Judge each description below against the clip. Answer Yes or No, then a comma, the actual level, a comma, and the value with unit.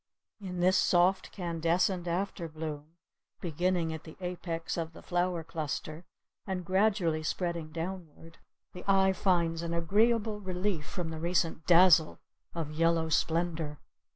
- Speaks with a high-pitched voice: No, medium, 170 Hz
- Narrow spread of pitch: Yes, narrow, 2.2 semitones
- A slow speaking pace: Yes, slow, 125 wpm